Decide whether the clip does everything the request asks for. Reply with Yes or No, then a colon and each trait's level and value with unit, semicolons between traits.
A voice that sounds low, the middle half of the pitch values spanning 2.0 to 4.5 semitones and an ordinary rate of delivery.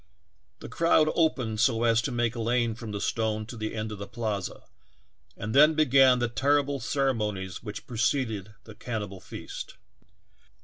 Yes: low, 115 Hz; average, 3.5 semitones; average, 170 wpm